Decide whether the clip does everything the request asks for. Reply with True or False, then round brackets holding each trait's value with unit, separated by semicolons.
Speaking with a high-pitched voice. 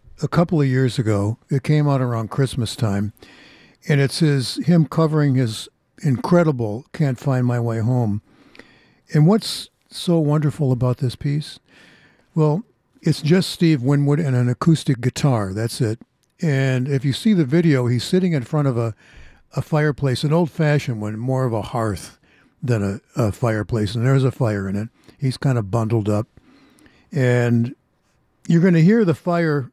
False (135 Hz)